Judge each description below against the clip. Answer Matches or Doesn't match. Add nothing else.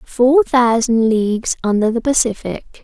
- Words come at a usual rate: Doesn't match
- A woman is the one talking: Matches